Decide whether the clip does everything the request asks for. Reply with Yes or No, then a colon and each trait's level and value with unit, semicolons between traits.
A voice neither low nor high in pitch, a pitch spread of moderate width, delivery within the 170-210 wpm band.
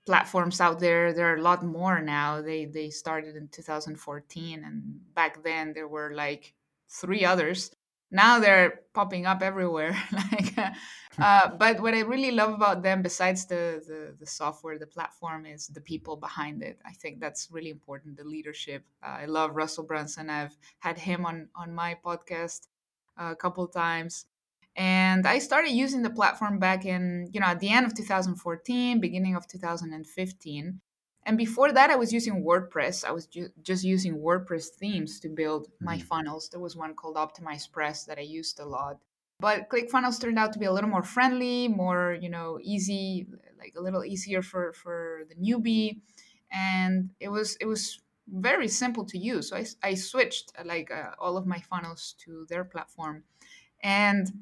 Yes: medium, 175 Hz; average, 3.9 semitones; average, 180 wpm